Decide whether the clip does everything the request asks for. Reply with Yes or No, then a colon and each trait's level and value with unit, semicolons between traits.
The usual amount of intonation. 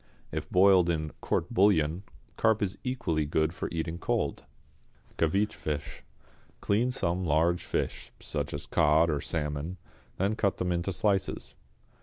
Yes: average, 3.9 semitones